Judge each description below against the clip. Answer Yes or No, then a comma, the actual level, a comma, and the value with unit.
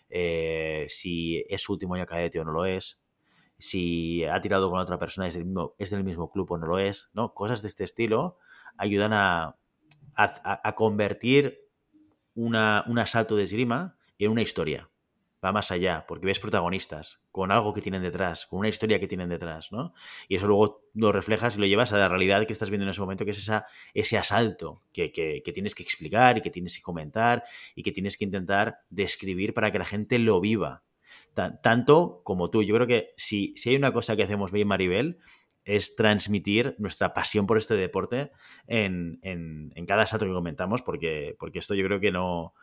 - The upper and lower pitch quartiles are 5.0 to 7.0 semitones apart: No, average, 3.0 semitones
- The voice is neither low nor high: No, low, 100 Hz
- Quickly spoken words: Yes, fast, 205 wpm